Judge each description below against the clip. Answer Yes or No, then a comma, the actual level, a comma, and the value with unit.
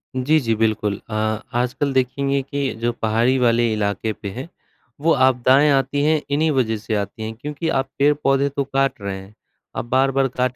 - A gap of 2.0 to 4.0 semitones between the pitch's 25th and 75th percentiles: Yes, average, 3.7 semitones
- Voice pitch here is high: No, low, 130 Hz